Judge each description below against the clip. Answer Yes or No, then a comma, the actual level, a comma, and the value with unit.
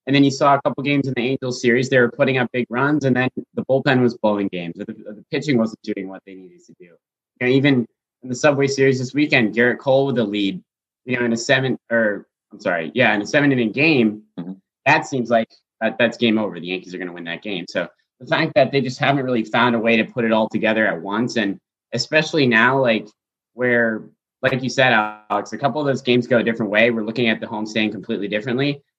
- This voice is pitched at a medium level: No, low, 120 Hz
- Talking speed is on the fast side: Yes, fast, 240 wpm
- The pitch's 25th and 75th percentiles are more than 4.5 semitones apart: No, average, 3.5 semitones